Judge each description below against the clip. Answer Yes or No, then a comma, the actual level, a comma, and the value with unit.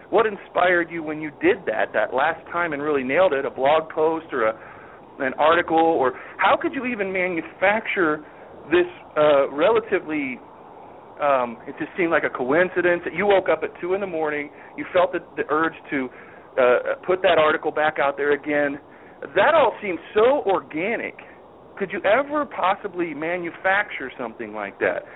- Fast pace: No, average, 175 wpm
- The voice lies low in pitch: No, medium, 175 Hz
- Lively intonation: No, average, 4.8 semitones